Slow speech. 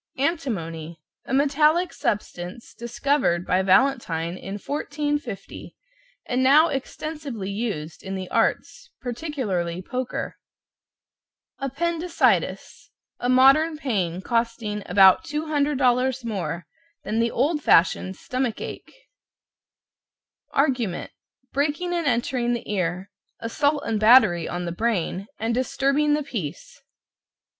Yes: slow, 105 wpm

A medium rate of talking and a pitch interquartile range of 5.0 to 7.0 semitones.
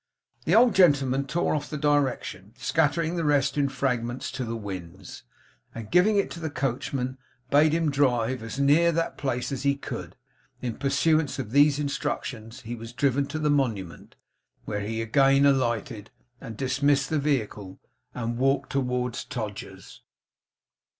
No: average, 155 wpm; average, 3.7 semitones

